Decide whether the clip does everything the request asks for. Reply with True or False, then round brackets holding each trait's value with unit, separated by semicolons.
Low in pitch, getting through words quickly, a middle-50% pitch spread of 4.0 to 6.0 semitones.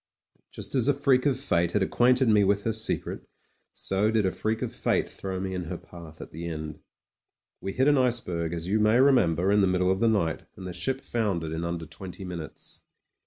True (95 Hz; 215 wpm; 5.1 semitones)